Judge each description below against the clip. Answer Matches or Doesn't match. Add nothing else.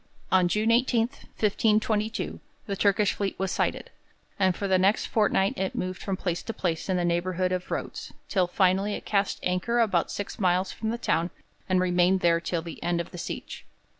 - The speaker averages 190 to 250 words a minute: Matches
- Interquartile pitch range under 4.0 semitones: Matches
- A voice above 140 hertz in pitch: Matches